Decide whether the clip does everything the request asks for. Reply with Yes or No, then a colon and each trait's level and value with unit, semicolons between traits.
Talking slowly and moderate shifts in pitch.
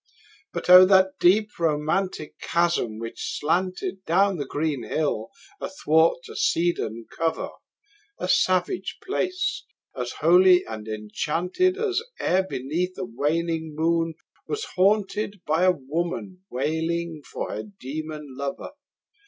Yes: slow, 120 wpm; average, 3.8 semitones